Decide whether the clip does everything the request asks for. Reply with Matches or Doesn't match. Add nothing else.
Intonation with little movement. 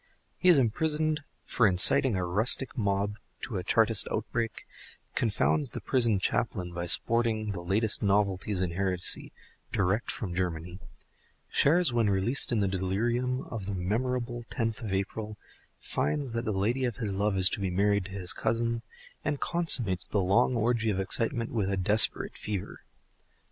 Doesn't match